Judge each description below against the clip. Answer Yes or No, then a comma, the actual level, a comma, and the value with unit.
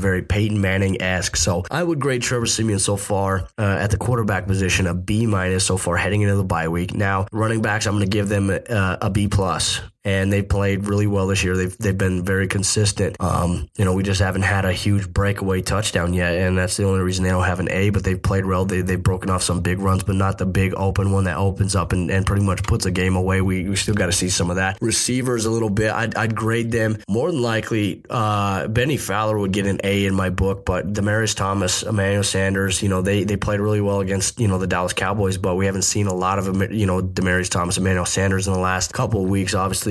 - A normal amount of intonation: No, narrow, 1.8 semitones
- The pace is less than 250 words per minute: No, fast, 255 wpm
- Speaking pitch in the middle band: No, very low, 95 Hz